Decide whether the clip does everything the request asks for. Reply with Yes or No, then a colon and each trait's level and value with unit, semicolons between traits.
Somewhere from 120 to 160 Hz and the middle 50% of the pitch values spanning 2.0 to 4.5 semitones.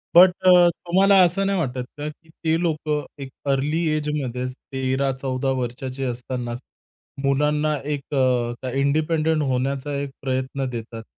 Yes: medium, 140 Hz; average, 3.3 semitones